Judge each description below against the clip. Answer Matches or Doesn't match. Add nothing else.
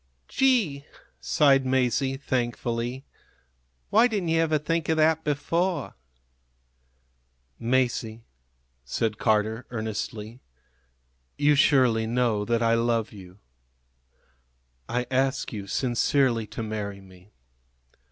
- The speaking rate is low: Matches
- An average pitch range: Matches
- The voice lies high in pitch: Doesn't match